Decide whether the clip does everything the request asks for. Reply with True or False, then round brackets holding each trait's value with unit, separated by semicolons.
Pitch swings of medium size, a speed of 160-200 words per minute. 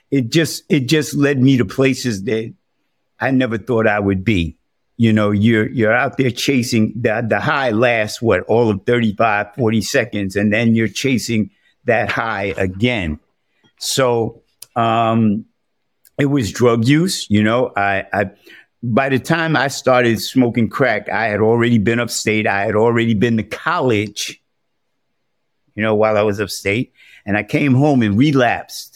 True (3.3 semitones; 165 wpm)